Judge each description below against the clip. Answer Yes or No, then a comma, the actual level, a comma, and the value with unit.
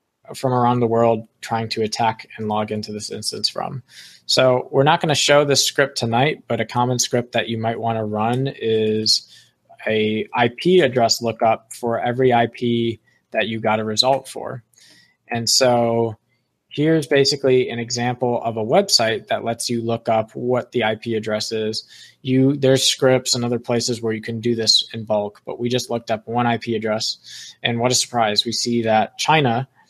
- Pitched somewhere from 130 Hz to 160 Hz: No, low, 115 Hz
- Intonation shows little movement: Yes, narrow, 2.0 semitones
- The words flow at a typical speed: Yes, average, 190 wpm